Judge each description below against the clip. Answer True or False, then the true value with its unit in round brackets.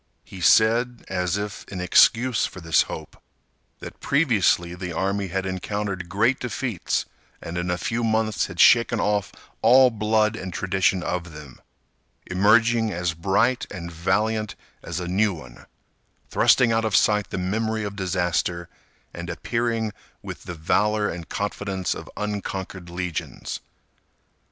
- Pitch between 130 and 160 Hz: False (100 Hz)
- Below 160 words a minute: True (140 wpm)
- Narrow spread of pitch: False (3.7 semitones)